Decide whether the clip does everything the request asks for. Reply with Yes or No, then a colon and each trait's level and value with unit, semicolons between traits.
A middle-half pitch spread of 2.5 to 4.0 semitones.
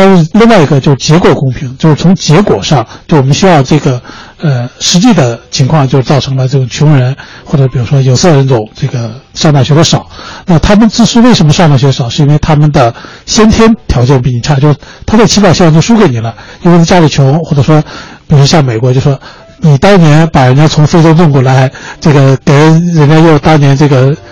Yes: average, 3.7 semitones